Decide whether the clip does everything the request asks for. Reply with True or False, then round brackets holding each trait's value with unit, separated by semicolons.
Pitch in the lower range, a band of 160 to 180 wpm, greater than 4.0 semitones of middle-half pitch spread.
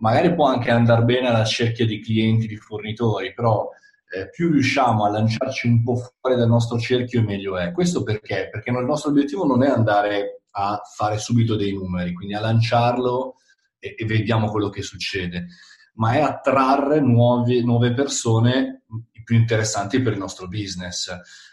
False (115 Hz; 165 wpm; 2.9 semitones)